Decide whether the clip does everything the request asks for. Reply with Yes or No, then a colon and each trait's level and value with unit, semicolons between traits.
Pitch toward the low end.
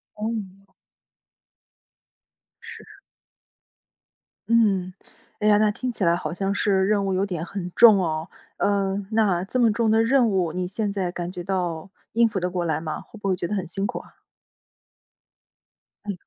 No: high, 195 Hz